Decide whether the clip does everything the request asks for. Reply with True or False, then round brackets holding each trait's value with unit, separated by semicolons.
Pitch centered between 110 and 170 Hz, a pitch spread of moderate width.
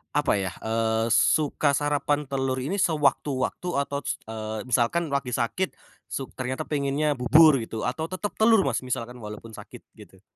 True (135 Hz; 4.2 semitones)